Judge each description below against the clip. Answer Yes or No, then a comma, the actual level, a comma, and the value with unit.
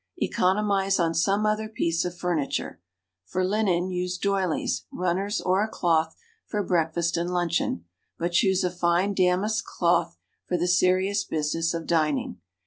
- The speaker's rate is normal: Yes, average, 145 wpm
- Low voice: No, medium, 180 Hz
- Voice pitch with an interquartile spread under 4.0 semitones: Yes, narrow, 2.5 semitones